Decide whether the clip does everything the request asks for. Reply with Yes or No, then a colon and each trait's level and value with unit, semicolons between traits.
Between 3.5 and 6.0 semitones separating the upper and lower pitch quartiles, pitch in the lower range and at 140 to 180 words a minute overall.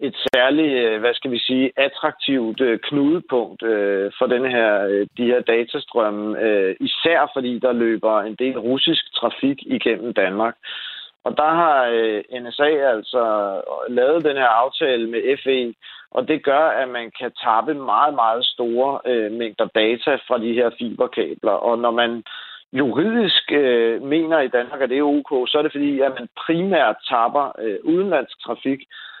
Yes: average, 3.9 semitones; low, 125 Hz; average, 150 wpm